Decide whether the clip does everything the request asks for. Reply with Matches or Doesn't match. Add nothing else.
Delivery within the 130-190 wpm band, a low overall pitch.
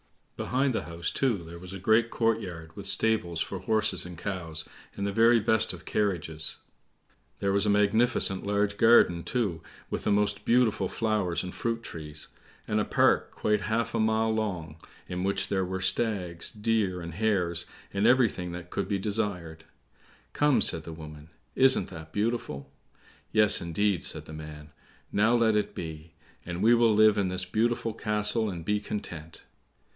Matches